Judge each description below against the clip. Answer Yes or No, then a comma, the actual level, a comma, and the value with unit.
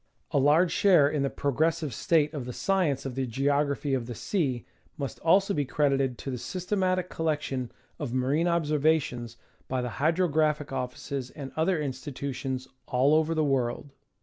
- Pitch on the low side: No, medium, 145 Hz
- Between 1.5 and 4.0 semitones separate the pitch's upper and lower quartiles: Yes, average, 3.3 semitones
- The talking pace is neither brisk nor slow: Yes, average, 160 wpm